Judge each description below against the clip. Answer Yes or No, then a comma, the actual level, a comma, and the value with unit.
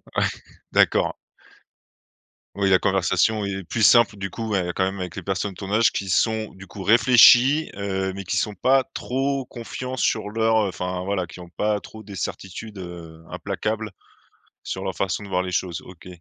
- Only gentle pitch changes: No, average, 3.1 semitones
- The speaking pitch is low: Yes, low, 100 Hz